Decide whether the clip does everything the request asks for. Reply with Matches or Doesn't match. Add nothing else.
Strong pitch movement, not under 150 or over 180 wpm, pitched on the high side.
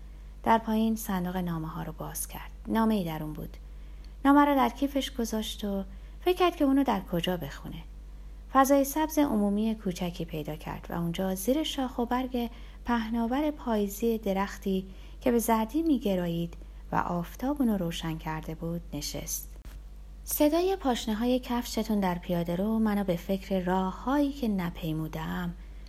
Matches